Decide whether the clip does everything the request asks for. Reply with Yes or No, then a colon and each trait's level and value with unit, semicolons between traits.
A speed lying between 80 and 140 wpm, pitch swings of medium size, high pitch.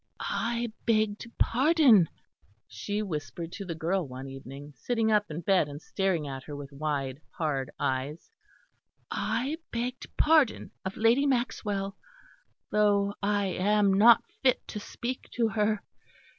No: slow, 135 wpm; wide, 7.2 semitones; high, 200 Hz